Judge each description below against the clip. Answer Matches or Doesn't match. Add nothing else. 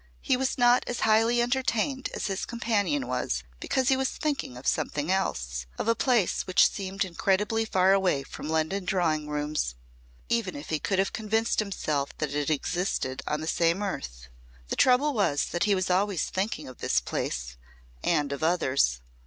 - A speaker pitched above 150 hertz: Matches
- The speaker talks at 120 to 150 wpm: Doesn't match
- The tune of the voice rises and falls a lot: Matches